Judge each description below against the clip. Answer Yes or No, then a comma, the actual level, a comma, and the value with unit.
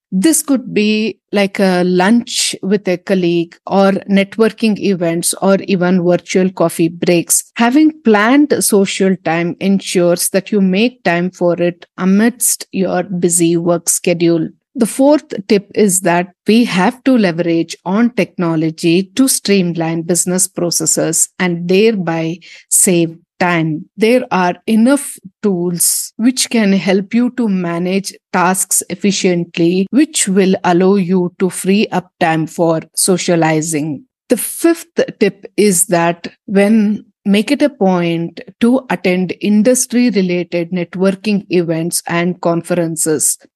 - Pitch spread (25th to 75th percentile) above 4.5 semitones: No, average, 3.7 semitones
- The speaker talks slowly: Yes, slow, 125 wpm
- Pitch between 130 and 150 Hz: No, high, 190 Hz